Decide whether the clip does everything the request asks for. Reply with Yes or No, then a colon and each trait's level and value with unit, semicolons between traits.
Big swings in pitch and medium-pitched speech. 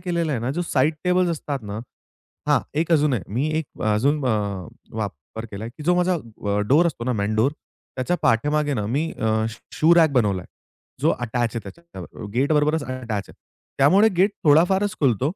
Yes: wide, 6.1 semitones; medium, 145 Hz